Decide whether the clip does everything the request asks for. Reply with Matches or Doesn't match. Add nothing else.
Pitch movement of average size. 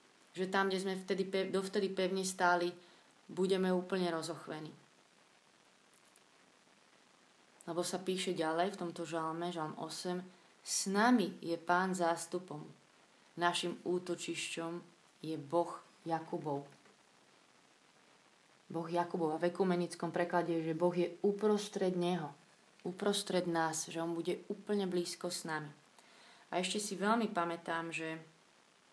Doesn't match